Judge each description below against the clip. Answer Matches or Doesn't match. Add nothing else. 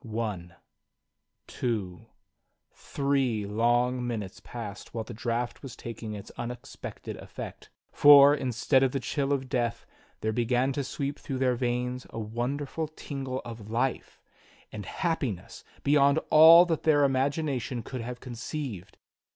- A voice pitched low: Matches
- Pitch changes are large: Doesn't match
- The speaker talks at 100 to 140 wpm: Matches